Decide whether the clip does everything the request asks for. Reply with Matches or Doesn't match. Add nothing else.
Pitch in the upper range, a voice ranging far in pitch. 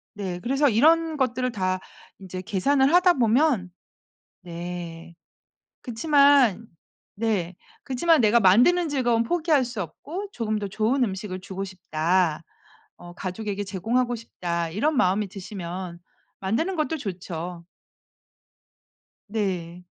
Matches